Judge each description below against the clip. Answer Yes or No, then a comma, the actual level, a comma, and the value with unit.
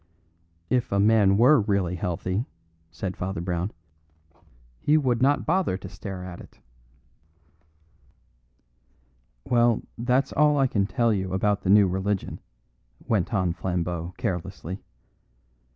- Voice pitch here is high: No, low, 100 Hz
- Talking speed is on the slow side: Yes, slow, 120 wpm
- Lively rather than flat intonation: No, average, 4.5 semitones